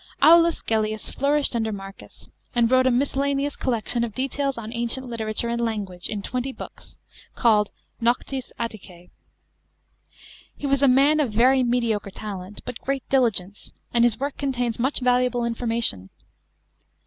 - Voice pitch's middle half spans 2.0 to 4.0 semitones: Yes, average, 3.5 semitones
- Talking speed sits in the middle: Yes, average, 155 wpm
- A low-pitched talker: No, high, 240 Hz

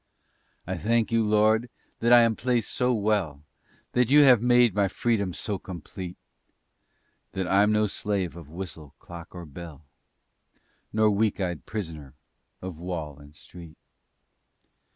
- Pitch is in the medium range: No, low, 100 Hz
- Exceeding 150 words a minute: No, average, 140 wpm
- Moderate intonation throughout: Yes, average, 4.5 semitones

